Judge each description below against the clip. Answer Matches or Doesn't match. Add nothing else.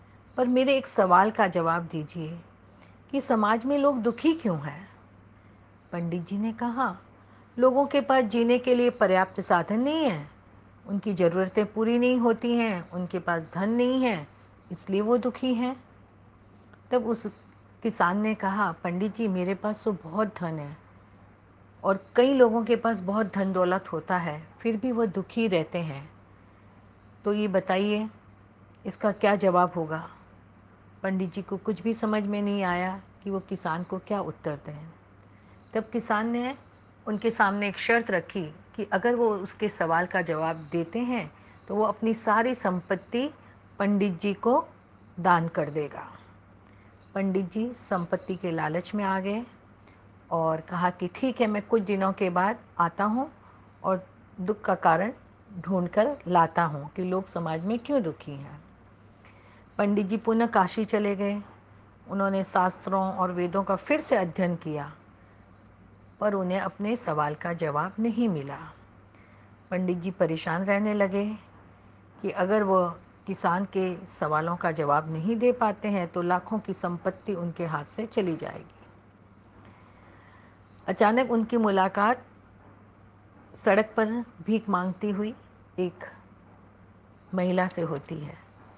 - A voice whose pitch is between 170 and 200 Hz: Matches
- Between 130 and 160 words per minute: Matches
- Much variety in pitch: Matches